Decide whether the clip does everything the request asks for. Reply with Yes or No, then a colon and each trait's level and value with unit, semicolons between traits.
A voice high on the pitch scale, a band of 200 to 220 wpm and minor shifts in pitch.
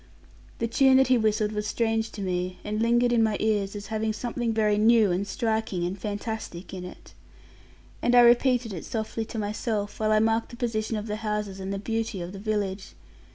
Yes: high, 215 Hz; fast, 205 wpm; narrow, 2.0 semitones